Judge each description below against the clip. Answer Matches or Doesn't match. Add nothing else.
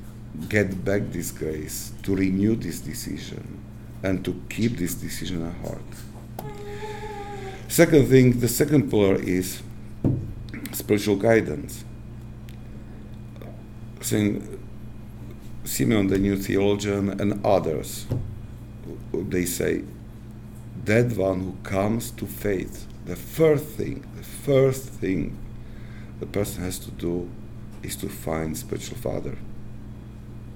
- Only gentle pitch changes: Matches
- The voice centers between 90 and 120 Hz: Matches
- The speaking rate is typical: Doesn't match